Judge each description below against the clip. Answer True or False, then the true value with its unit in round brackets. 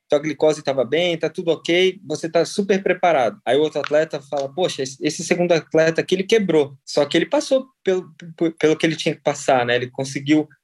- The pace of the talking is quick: True (215 wpm)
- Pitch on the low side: False (160 Hz)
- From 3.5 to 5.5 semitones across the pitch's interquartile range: False (2.9 semitones)